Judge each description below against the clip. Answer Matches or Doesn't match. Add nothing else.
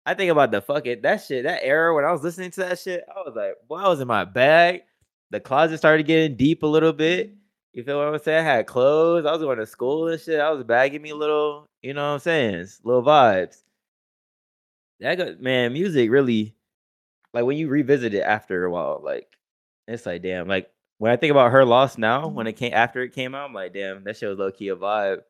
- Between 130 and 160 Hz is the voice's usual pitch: Matches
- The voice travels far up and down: Matches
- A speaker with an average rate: Doesn't match